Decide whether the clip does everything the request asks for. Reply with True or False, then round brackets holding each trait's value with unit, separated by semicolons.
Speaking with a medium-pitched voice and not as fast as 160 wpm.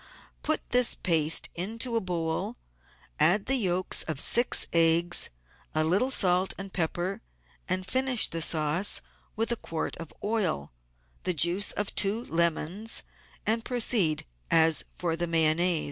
True (180 Hz; 140 wpm)